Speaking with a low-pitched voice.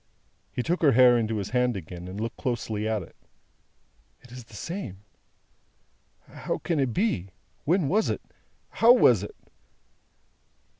Yes: low, 120 Hz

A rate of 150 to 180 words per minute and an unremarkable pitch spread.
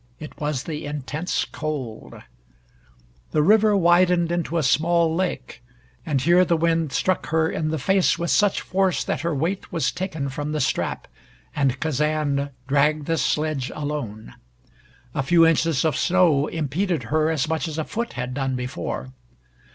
Yes: average, 160 wpm; average, 3.2 semitones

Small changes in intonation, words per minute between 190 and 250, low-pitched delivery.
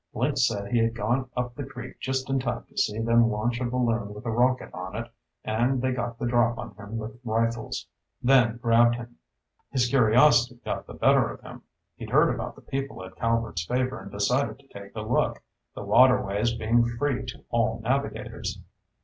Yes: narrow, 2.1 semitones; average, 195 wpm; low, 120 Hz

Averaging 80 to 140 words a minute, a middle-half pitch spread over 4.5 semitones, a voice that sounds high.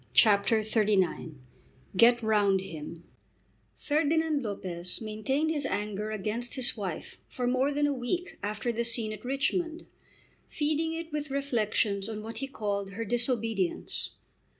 Yes: slow, 135 wpm; average, 5.2 semitones; high, 230 Hz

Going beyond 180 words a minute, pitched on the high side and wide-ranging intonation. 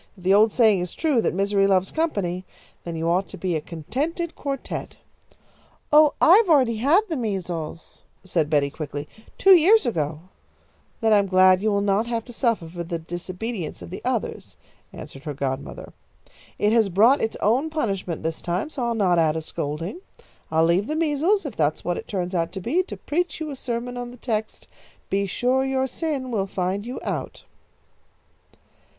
Yes: average, 190 wpm; high, 205 Hz; wide, 7.1 semitones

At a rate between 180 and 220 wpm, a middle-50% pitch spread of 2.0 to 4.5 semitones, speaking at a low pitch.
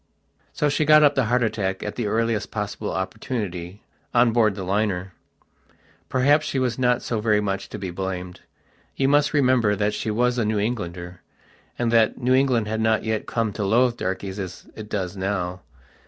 Yes: average, 185 wpm; average, 4.0 semitones; low, 110 Hz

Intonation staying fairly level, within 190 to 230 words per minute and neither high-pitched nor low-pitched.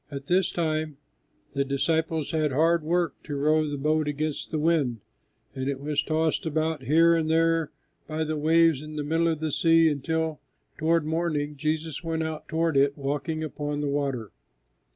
No: narrow, 1.8 semitones; average, 175 wpm; medium, 155 Hz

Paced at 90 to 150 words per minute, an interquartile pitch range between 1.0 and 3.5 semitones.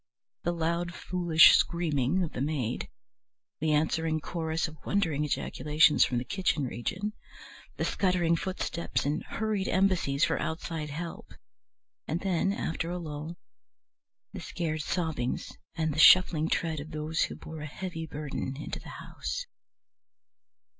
Yes: average, 140 wpm; narrow, 2.5 semitones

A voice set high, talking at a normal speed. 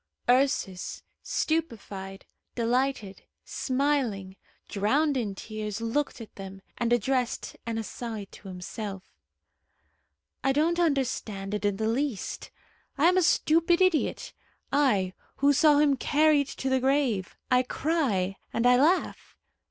No: very high, 250 Hz; slow, 125 wpm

